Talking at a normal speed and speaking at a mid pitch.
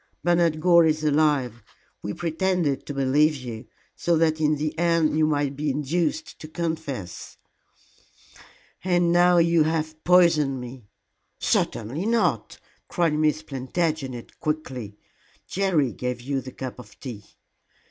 No: slow, 130 wpm; medium, 155 Hz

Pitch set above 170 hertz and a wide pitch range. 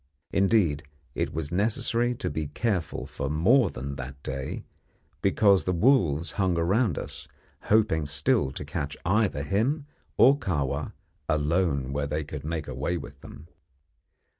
No: very low, 80 Hz; wide, 6.2 semitones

